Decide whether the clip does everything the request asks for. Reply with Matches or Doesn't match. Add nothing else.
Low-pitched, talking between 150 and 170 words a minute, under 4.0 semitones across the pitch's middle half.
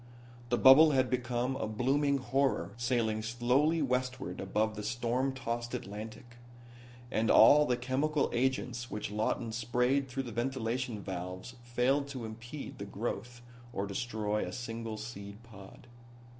Doesn't match